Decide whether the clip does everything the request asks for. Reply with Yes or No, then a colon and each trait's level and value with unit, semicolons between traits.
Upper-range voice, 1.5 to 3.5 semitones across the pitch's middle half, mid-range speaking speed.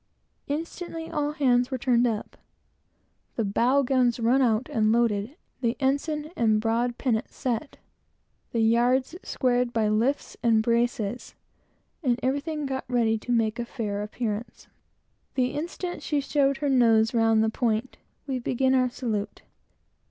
Yes: high, 245 Hz; average, 3.2 semitones; average, 145 wpm